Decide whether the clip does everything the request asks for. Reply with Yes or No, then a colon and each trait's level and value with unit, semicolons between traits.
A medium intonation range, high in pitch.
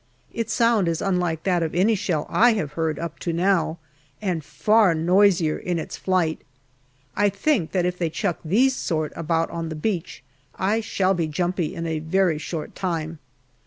No: average, 3.3 semitones; medium, 175 Hz